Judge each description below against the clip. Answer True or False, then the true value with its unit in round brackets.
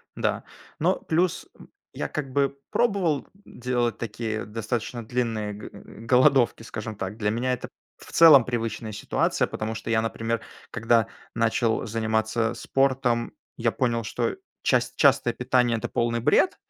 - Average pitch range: False (2.3 semitones)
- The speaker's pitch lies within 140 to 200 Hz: False (115 Hz)